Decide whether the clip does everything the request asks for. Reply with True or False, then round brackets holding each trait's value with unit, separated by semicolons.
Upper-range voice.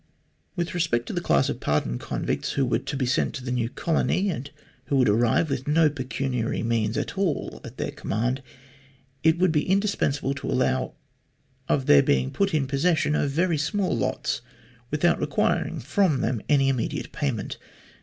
False (140 Hz)